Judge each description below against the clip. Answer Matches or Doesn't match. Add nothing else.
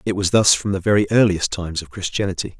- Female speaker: Doesn't match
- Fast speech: Matches